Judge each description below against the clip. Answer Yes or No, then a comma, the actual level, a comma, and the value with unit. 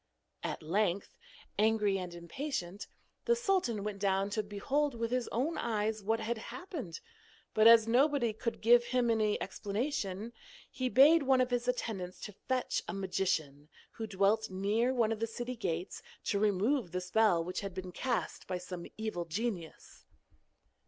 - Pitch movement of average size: Yes, average, 4.0 semitones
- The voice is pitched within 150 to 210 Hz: No, high, 220 Hz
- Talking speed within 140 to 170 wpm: Yes, average, 160 wpm